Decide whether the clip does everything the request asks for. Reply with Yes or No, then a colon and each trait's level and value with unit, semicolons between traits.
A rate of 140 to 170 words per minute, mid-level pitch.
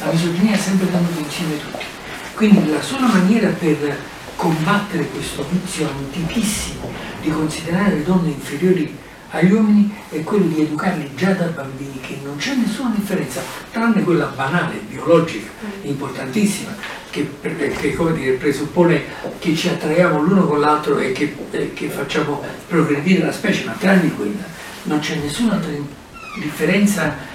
Yes: average, 145 wpm; medium, 170 Hz